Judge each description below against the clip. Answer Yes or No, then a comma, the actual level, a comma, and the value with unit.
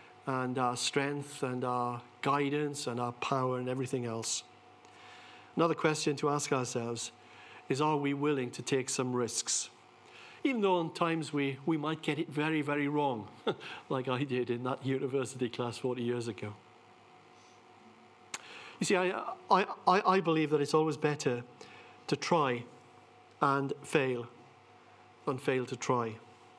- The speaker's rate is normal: Yes, average, 145 wpm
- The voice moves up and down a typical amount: Yes, average, 3.4 semitones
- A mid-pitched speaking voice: No, low, 130 Hz